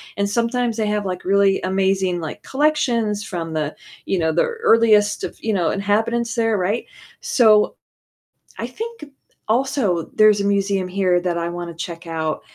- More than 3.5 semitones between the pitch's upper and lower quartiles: Yes, average, 4.1 semitones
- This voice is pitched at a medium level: No, high, 200 Hz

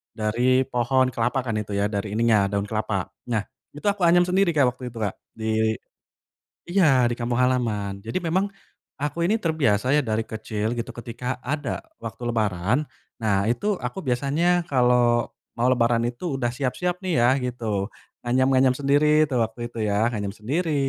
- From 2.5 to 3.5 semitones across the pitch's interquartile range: No, average, 3.9 semitones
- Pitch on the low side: Yes, low, 120 Hz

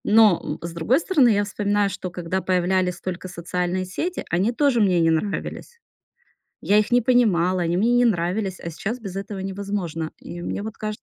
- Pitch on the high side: Yes, high, 195 Hz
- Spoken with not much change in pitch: No, average, 3.6 semitones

